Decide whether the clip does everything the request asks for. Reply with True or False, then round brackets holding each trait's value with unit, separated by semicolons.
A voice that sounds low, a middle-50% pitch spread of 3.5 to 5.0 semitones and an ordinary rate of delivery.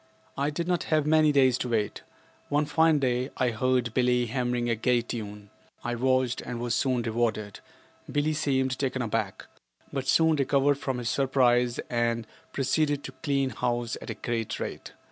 False (125 Hz; 2.8 semitones; 170 wpm)